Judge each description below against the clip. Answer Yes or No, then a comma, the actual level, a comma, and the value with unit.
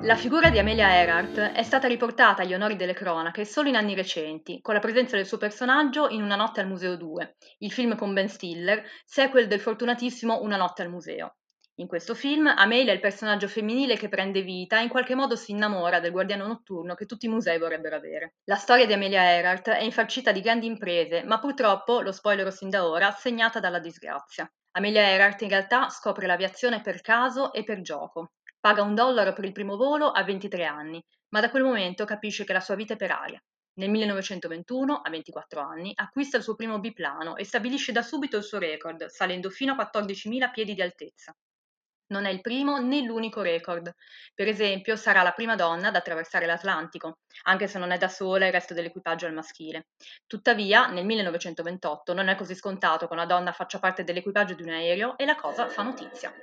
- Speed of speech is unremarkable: No, fast, 205 wpm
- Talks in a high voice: Yes, high, 200 Hz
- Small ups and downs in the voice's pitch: No, average, 4.2 semitones